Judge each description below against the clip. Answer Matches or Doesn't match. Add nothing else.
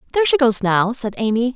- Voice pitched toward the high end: Matches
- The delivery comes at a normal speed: Doesn't match